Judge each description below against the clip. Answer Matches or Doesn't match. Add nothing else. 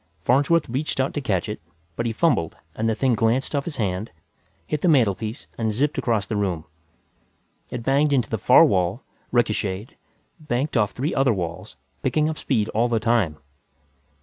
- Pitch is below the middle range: Matches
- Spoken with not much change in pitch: Doesn't match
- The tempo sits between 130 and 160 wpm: Doesn't match